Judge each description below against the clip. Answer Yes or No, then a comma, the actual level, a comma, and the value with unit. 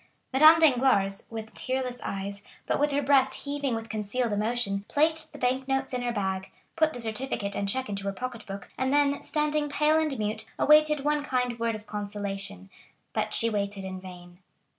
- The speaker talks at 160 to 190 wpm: Yes, average, 185 wpm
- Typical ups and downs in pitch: No, wide, 5.9 semitones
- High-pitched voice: Yes, high, 245 Hz